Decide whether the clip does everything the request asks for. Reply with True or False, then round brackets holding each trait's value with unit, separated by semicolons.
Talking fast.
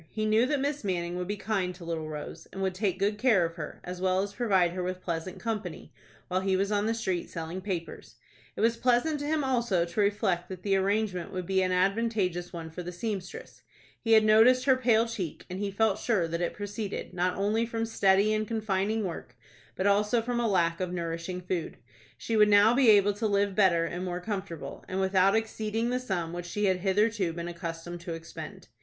True (220 wpm)